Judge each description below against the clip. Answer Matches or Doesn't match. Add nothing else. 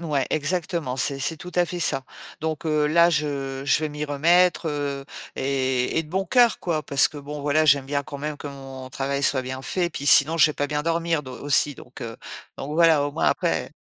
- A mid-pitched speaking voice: Matches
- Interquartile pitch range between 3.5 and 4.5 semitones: Doesn't match